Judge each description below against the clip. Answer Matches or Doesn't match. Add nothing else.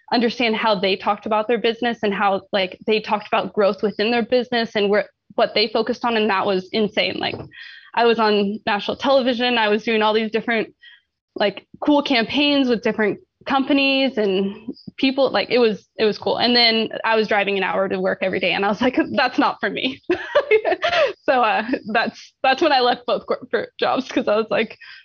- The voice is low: Doesn't match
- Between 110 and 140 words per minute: Doesn't match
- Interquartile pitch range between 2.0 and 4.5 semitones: Matches